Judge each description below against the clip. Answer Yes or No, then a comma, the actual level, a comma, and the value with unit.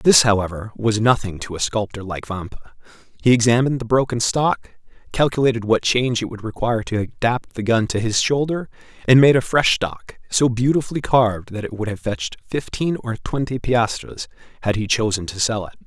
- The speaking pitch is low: Yes, low, 115 Hz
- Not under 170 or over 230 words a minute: Yes, average, 190 wpm